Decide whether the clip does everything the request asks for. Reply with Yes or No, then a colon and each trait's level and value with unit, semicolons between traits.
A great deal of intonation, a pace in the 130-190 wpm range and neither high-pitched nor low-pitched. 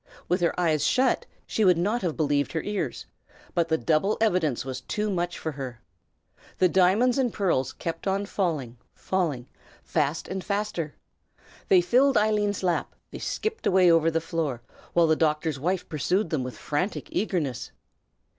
No: average, 4.5 semitones; average, 165 wpm; medium, 175 Hz